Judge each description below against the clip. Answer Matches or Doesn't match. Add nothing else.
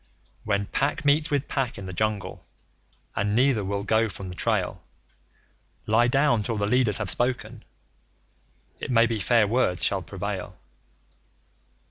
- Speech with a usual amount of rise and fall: Matches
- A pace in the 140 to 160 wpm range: Matches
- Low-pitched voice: Matches